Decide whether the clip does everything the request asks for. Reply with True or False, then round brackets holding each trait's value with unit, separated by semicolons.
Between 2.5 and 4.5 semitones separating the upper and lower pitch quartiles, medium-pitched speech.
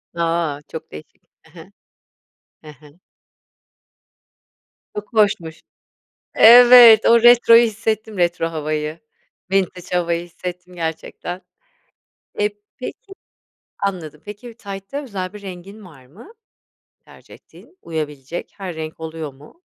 False (5.1 semitones; 180 Hz)